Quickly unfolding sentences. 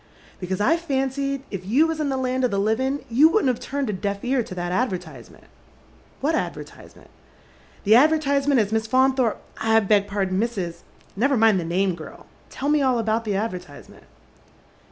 Yes: fast, 215 wpm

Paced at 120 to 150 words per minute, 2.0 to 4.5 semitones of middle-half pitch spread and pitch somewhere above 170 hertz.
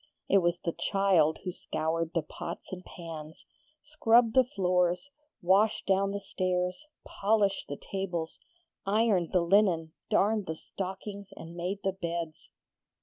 Yes: average, 140 wpm; average, 2.9 semitones; medium, 185 Hz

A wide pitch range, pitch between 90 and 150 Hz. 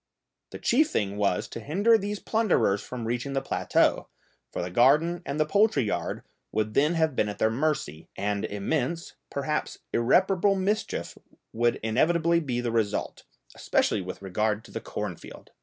Yes: wide, 7.8 semitones; low, 135 Hz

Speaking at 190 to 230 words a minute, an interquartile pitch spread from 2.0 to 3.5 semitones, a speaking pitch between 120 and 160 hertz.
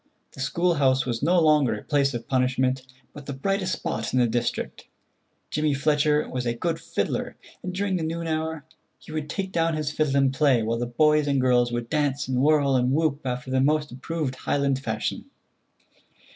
Yes: average, 195 wpm; average, 3.2 semitones; medium, 140 Hz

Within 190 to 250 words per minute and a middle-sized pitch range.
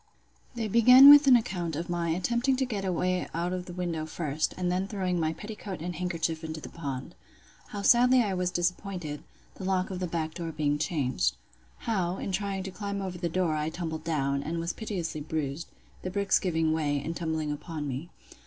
Yes: average, 200 wpm; average, 3.3 semitones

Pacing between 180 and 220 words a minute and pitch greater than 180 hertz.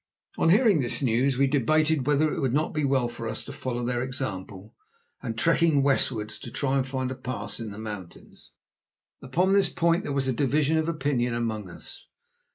No: average, 190 wpm; low, 130 Hz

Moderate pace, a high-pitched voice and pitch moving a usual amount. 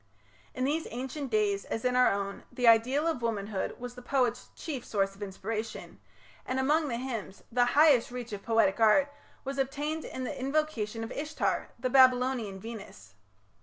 Yes: average, 170 wpm; high, 245 Hz; average, 3.5 semitones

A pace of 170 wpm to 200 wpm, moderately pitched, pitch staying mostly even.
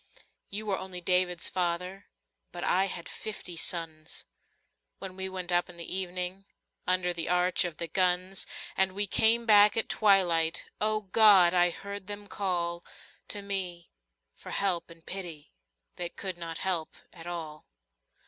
No: average, 160 wpm; medium, 180 Hz; narrow, 2.2 semitones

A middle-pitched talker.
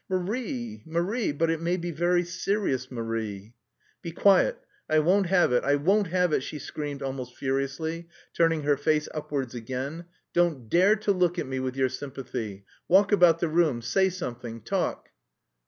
Yes: medium, 160 Hz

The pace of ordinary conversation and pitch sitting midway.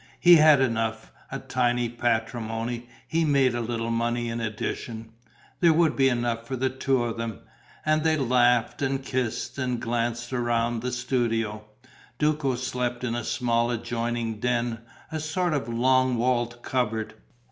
No: average, 155 wpm; low, 120 Hz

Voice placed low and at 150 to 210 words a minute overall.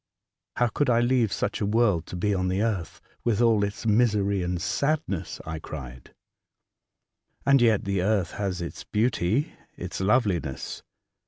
Yes: low, 100 Hz; average, 170 wpm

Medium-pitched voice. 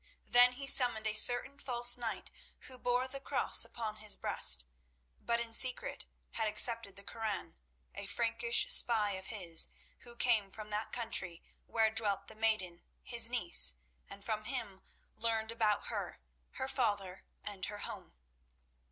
No: high, 225 Hz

